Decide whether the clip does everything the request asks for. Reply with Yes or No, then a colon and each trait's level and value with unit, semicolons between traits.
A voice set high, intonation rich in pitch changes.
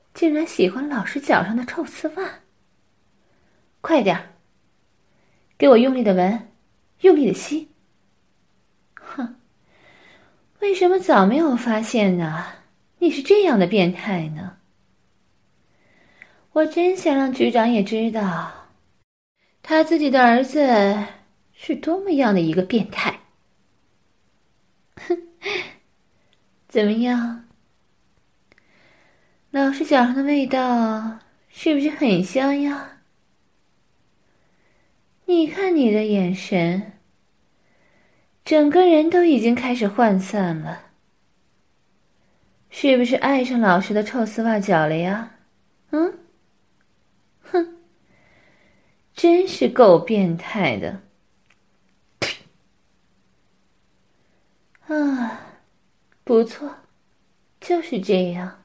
Yes: very high, 250 Hz; wide, 7.0 semitones